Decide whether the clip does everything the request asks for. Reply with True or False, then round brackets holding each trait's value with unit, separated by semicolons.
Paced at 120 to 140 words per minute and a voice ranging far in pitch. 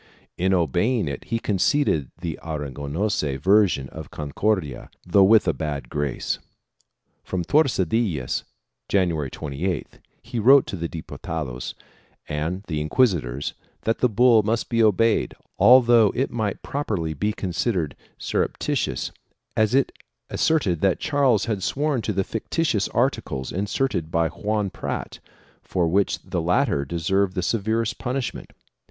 True (135 wpm; 6.1 semitones)